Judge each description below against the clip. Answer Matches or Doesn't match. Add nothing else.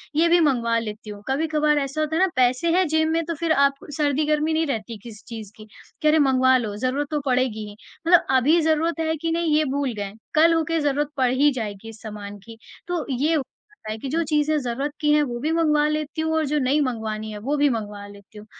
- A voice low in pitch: Doesn't match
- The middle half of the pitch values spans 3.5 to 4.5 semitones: Doesn't match